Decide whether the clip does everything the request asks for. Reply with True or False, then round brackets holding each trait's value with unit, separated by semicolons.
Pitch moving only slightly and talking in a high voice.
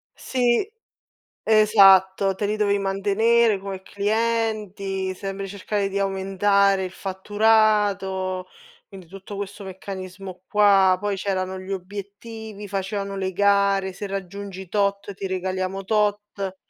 True (1.4 semitones; 195 Hz)